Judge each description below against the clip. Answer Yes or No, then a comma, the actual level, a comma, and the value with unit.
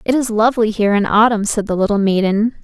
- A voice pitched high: Yes, high, 215 Hz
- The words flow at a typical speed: No, fast, 225 wpm